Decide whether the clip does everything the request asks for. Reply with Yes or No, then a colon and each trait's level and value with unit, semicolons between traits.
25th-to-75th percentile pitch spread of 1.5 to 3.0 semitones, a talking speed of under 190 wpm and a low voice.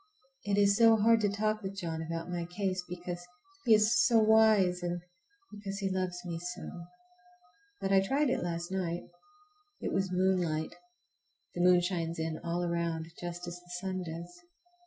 No: narrow, 2.6 semitones; average, 170 wpm; medium, 180 Hz